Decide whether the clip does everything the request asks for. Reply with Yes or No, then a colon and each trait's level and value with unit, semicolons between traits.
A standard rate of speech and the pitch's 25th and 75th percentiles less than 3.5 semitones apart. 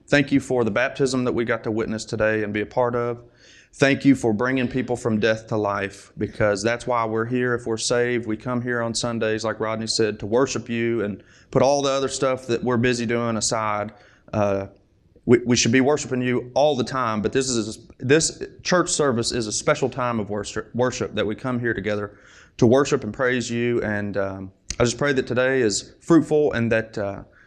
No: fast, 220 wpm; average, 2.7 semitones